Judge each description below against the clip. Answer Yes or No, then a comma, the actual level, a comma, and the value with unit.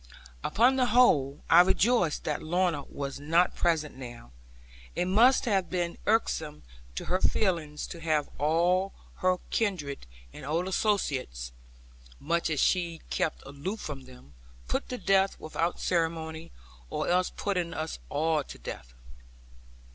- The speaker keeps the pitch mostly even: No, average, 4.0 semitones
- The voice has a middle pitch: Yes, medium, 165 Hz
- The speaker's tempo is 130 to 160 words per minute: Yes, average, 140 wpm